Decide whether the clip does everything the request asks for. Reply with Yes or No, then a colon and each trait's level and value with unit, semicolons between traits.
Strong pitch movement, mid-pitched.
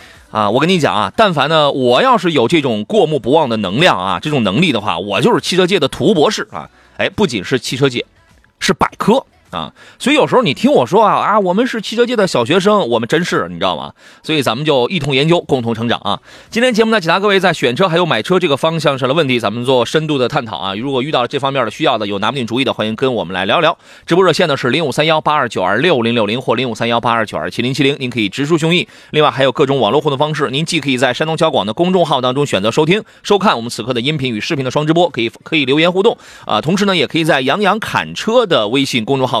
Yes: wide, 6.2 semitones; medium, 145 Hz